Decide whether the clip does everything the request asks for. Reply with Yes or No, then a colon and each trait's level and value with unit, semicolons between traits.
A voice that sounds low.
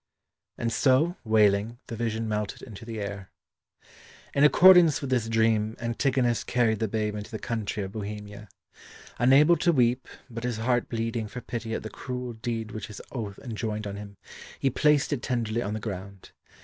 Yes: low, 115 Hz